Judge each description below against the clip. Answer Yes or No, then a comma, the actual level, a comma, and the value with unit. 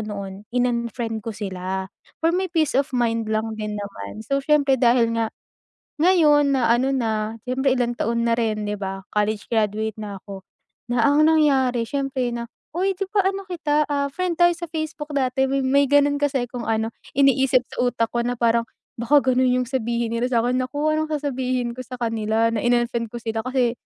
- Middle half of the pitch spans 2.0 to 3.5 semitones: No, average, 3.9 semitones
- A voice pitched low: No, high, 245 Hz